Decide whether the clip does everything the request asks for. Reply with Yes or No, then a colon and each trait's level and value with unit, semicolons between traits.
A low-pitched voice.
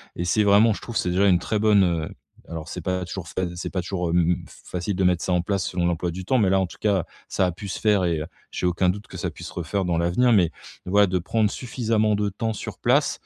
Yes: very low, 95 Hz